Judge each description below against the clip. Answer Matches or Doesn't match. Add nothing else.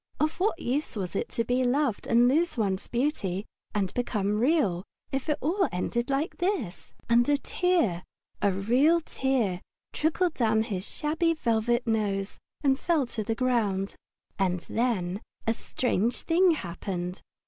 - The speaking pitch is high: Matches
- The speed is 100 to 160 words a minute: Matches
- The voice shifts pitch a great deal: Matches